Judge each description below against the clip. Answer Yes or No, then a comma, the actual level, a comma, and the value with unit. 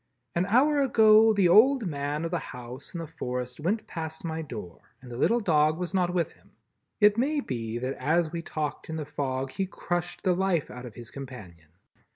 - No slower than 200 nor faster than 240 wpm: Yes, fast, 205 wpm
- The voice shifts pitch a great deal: Yes, wide, 6.6 semitones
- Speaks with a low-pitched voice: No, medium, 160 Hz